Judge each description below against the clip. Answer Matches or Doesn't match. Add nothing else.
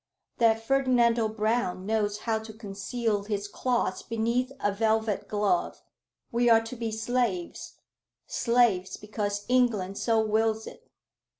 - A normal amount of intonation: Doesn't match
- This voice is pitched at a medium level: Doesn't match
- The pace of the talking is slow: Matches